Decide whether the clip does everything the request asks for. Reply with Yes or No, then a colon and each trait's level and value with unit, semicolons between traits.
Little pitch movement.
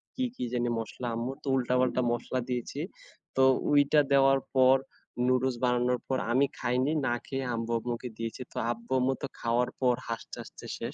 Yes: narrow, 1.7 semitones